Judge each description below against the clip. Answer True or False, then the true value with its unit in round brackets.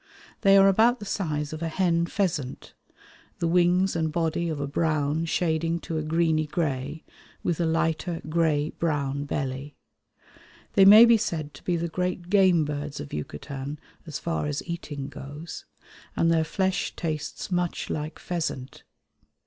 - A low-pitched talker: False (160 Hz)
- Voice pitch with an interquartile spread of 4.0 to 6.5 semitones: False (2.9 semitones)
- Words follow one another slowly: False (155 wpm)